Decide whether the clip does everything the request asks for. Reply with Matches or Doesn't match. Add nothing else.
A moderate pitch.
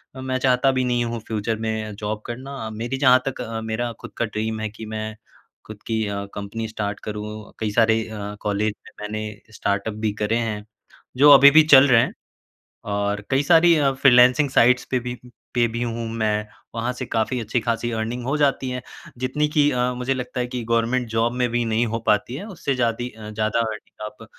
Doesn't match